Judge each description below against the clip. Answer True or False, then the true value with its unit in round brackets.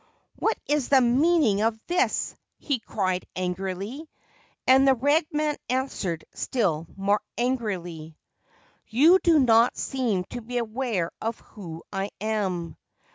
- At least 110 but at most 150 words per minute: True (140 wpm)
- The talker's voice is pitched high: True (230 Hz)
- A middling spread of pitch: False (5.7 semitones)